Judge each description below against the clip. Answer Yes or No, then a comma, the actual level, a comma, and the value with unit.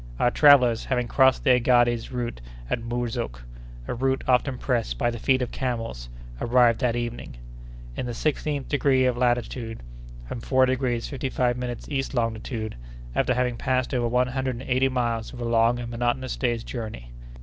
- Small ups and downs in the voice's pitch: Yes, narrow, 1.9 semitones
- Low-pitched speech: Yes, low, 120 Hz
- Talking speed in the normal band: Yes, average, 170 wpm